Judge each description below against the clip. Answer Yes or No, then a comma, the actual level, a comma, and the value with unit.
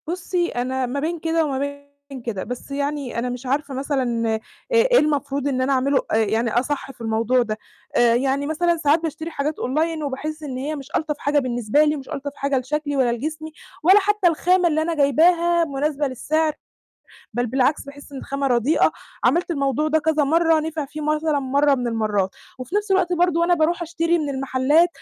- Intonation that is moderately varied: Yes, average, 3.4 semitones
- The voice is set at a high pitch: Yes, very high, 285 Hz